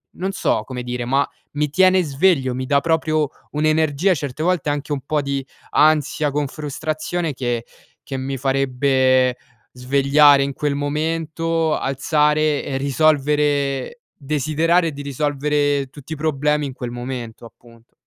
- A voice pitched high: No, medium, 145 Hz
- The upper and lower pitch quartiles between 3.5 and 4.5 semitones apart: No, narrow, 2.5 semitones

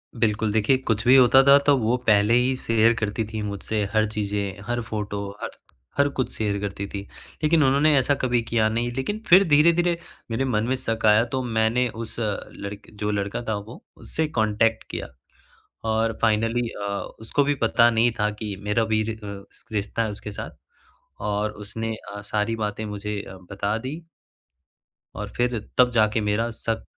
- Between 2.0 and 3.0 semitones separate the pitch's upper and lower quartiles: Yes, average, 2.7 semitones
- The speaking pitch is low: Yes, low, 110 Hz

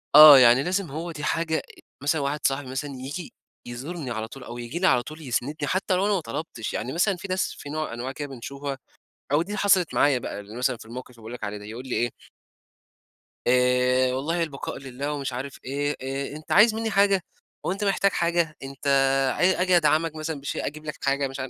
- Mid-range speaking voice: Yes, medium, 145 Hz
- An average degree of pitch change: Yes, average, 4.8 semitones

